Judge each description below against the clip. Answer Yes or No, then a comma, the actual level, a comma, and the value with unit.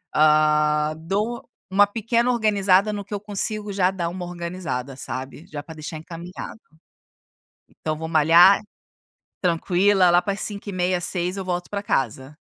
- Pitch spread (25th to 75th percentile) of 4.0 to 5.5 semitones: Yes, average, 4.3 semitones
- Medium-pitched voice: Yes, medium, 180 Hz